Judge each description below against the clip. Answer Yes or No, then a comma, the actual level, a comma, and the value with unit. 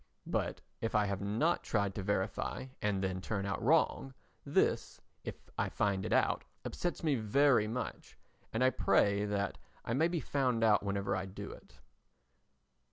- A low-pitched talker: Yes, low, 105 Hz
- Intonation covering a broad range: No, average, 4.6 semitones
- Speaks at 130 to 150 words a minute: No, average, 165 wpm